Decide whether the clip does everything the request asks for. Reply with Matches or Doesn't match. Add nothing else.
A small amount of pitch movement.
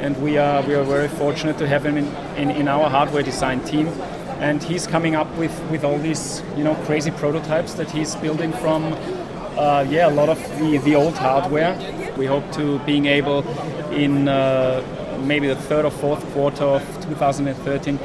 Matches